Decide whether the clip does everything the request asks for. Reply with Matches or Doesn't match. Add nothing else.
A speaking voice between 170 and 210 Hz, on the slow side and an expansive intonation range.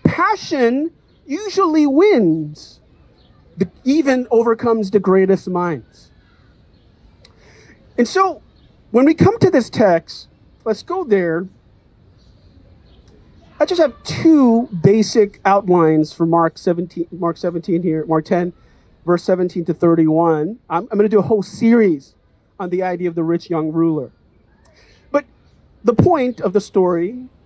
Matches